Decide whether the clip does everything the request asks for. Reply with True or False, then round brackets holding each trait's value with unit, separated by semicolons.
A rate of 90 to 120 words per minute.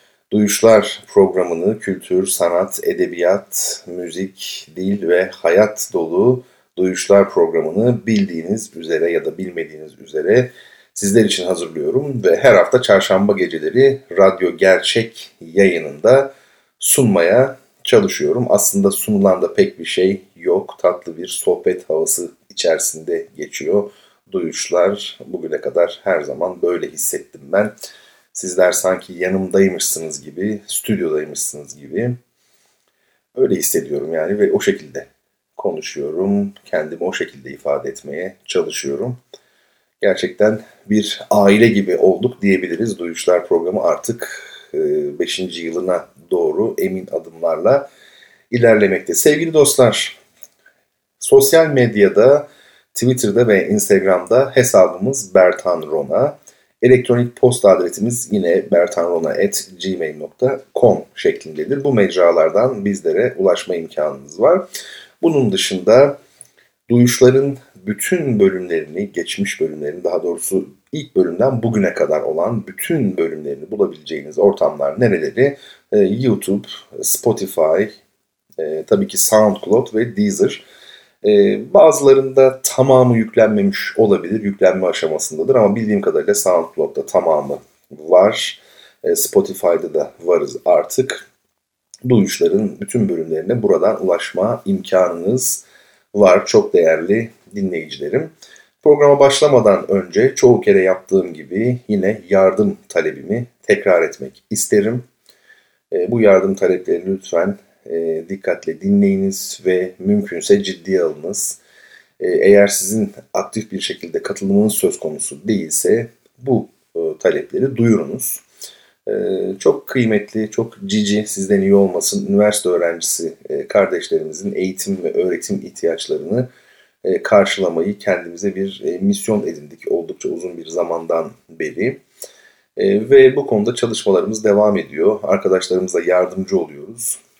True (105 wpm)